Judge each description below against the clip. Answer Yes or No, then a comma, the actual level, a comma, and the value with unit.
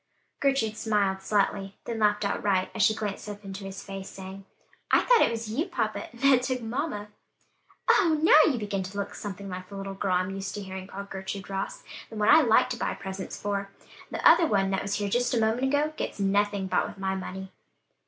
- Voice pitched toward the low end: No, high, 205 Hz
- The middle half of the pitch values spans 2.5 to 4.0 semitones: Yes, average, 2.8 semitones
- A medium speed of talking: No, fast, 215 wpm